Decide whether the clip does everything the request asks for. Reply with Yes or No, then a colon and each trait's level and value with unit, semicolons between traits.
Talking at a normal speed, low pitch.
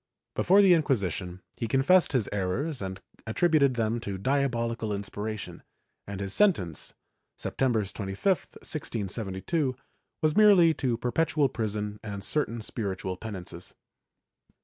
No: slow, 120 wpm; low, 115 Hz